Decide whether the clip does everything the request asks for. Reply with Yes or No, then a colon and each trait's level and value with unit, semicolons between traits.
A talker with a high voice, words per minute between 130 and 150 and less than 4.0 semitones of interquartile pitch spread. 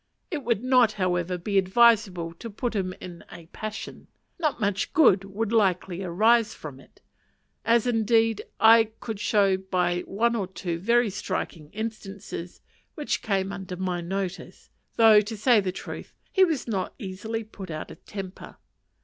No: high, 200 Hz; average, 165 wpm; average, 3.5 semitones